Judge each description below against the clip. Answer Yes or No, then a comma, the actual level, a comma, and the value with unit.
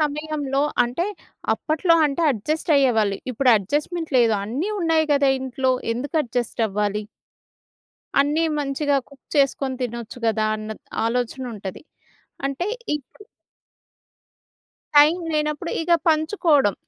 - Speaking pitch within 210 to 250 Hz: No, very high, 275 Hz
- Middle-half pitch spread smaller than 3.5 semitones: No, average, 4.5 semitones